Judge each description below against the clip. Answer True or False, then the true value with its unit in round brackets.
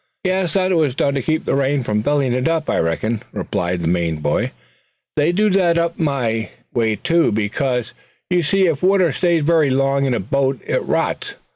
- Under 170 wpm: False (195 wpm)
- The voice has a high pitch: False (140 Hz)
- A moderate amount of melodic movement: False (6.4 semitones)